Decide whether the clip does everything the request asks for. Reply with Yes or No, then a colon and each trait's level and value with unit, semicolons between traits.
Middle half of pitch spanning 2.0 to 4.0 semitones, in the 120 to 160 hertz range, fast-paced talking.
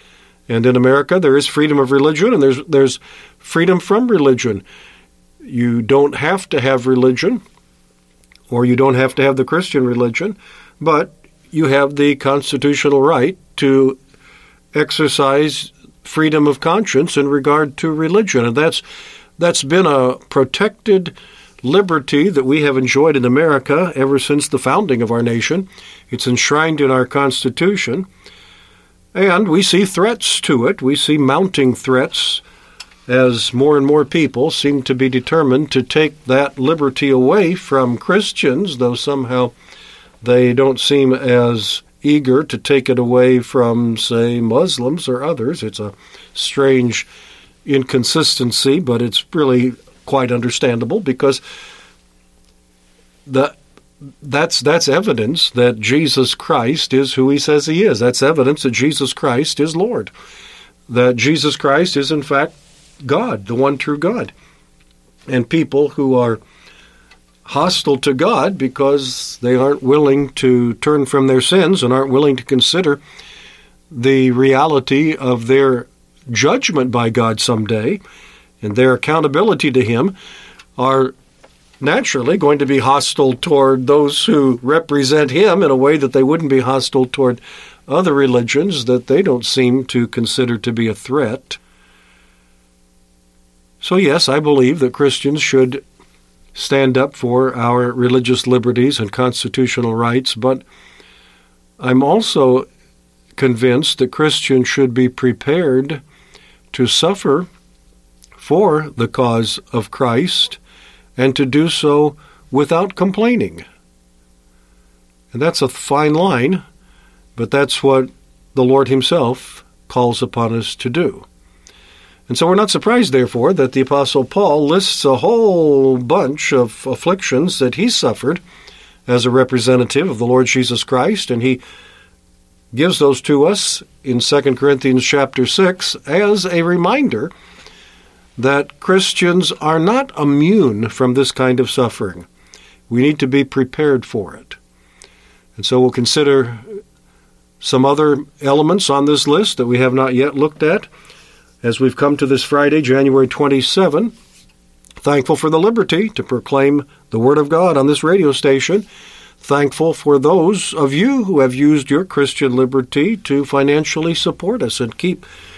No: average, 3.4 semitones; low, 135 Hz; average, 140 wpm